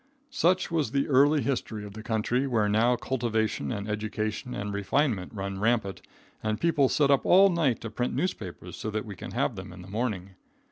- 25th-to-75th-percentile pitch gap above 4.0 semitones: Yes, average, 4.9 semitones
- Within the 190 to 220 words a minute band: Yes, average, 195 wpm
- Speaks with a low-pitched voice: Yes, low, 115 Hz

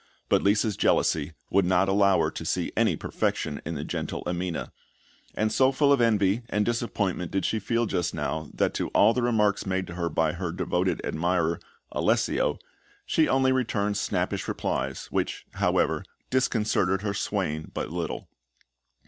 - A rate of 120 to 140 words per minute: No, average, 165 wpm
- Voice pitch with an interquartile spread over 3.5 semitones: Yes, average, 4.2 semitones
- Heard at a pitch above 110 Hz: No, very low, 95 Hz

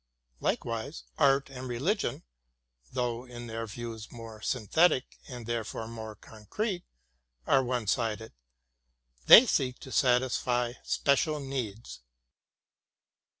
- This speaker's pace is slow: Yes, slow, 105 wpm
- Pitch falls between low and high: No, low, 120 Hz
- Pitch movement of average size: Yes, average, 3.1 semitones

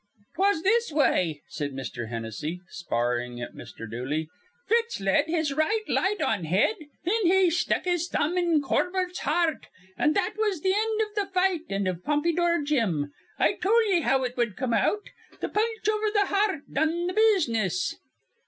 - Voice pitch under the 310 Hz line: No, very high, 320 Hz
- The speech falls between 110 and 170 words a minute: No, average, 180 wpm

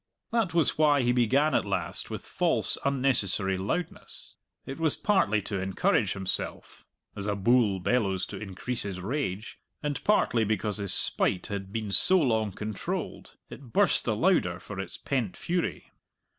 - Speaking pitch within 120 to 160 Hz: No, low, 110 Hz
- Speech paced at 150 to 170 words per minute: Yes, average, 155 wpm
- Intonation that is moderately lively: No, wide, 6.0 semitones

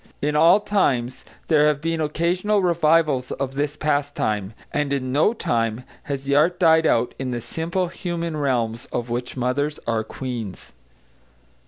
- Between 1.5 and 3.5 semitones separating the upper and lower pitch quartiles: No, average, 4.7 semitones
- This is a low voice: No, medium, 145 Hz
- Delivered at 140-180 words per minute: Yes, average, 155 wpm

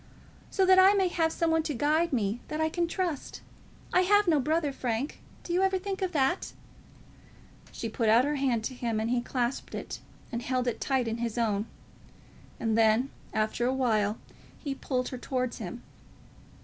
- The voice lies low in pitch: No, very high, 265 Hz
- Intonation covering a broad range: Yes, wide, 5.9 semitones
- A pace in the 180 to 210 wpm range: Yes, average, 190 wpm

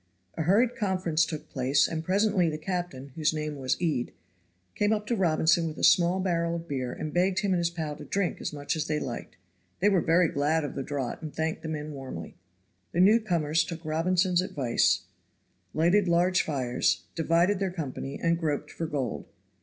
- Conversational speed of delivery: Yes, average, 195 wpm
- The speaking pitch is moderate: Yes, medium, 165 Hz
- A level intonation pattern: No, average, 3.4 semitones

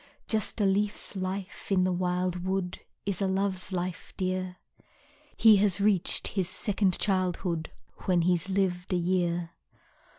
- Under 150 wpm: Yes, average, 140 wpm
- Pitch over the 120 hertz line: Yes, medium, 185 Hz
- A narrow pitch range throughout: Yes, narrow, 1.6 semitones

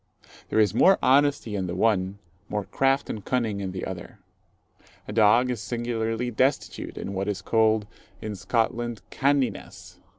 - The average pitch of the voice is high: No, low, 110 Hz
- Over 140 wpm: Yes, average, 155 wpm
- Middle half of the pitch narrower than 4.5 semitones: Yes, average, 3.6 semitones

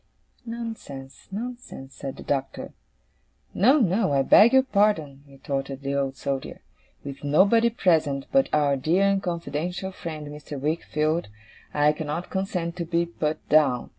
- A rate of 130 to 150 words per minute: Yes, average, 140 wpm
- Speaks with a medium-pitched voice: Yes, medium, 155 Hz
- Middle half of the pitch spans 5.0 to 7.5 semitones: Yes, wide, 5.6 semitones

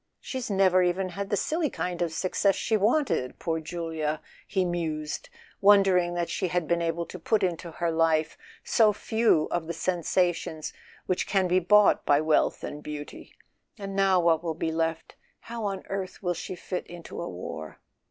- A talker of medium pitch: Yes, medium, 175 Hz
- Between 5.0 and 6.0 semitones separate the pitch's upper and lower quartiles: No, average, 3.2 semitones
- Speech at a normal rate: Yes, average, 180 wpm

